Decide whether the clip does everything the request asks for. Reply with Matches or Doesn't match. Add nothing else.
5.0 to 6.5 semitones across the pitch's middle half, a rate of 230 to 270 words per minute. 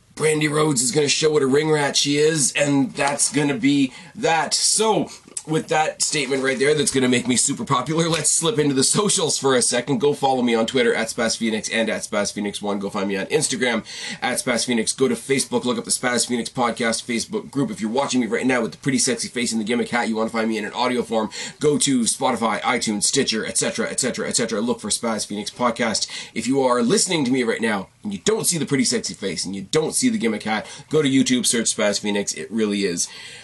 Matches